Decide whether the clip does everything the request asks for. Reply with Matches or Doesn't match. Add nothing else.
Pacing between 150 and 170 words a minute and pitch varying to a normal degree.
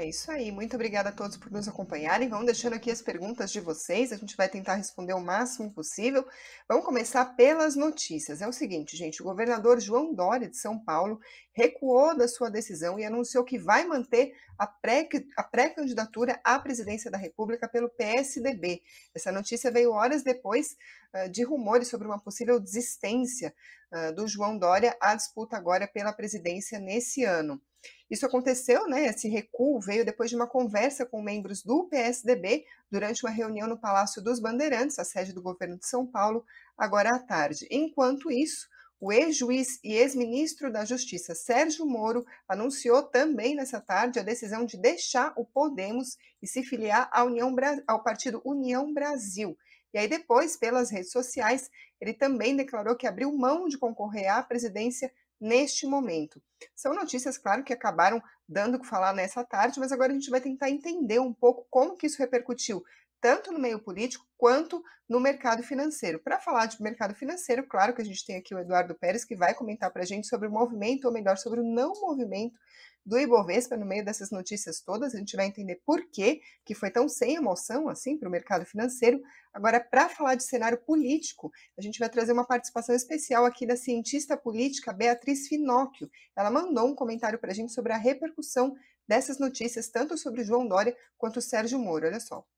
Doesn't match